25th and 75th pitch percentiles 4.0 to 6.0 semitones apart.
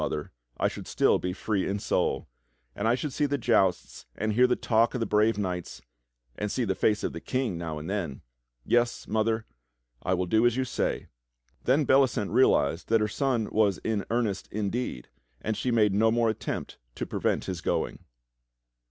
No: average, 3.6 semitones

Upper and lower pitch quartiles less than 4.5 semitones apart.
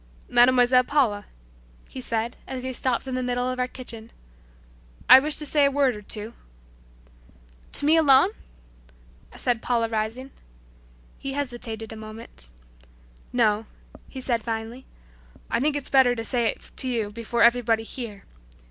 Yes: narrow, 2.6 semitones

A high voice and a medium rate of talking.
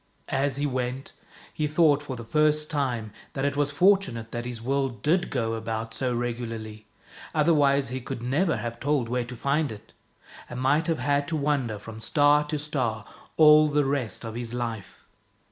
No: low, 135 Hz; average, 180 wpm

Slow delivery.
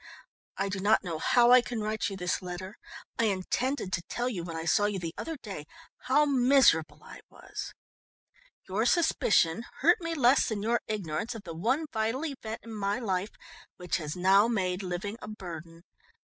No: average, 185 wpm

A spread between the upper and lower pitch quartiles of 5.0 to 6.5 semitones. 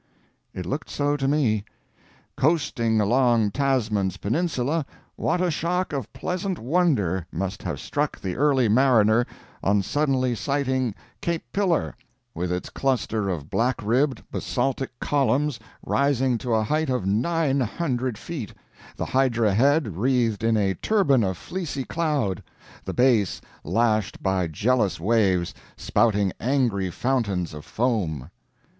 Yes: average, 5.3 semitones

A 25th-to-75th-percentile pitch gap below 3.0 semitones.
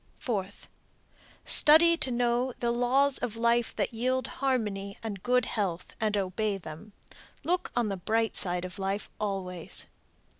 No: average, 4.0 semitones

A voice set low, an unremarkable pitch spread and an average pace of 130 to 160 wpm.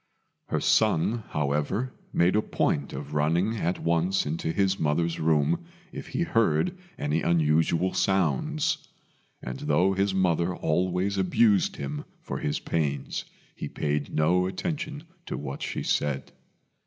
Yes: very low, 85 Hz; average, 4.6 semitones; slow, 135 wpm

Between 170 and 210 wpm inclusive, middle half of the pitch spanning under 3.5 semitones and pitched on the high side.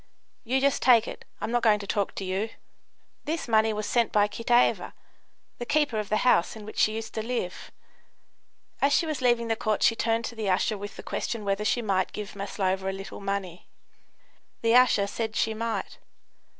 Yes: average, 200 wpm; average, 2.8 semitones; high, 220 Hz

